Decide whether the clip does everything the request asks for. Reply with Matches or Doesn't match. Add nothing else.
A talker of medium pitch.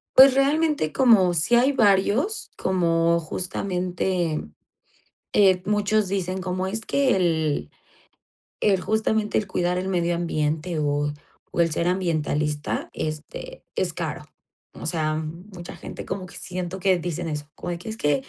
Matches